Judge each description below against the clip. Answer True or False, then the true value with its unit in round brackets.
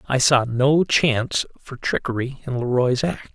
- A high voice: False (130 Hz)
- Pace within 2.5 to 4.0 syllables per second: False (4.3 syllables/s)